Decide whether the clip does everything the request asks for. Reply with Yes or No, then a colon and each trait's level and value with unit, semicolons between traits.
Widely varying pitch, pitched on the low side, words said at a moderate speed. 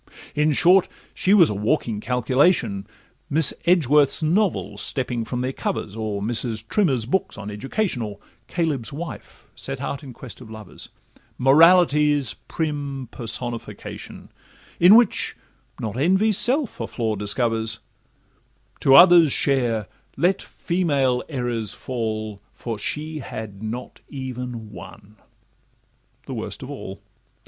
No: wide, 6.1 semitones; low, 130 Hz; slow, 120 wpm